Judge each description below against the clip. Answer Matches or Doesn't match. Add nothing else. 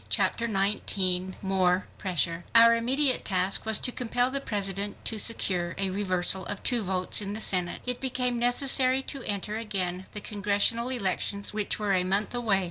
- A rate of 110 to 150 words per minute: Doesn't match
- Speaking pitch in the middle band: Doesn't match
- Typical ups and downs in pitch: Matches